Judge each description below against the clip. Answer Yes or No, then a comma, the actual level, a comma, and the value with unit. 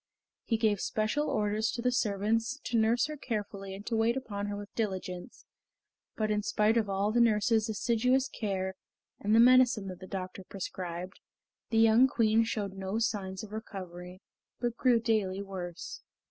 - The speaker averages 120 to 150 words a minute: No, average, 170 wpm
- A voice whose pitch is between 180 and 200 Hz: No, high, 215 Hz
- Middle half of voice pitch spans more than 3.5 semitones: No, average, 2.8 semitones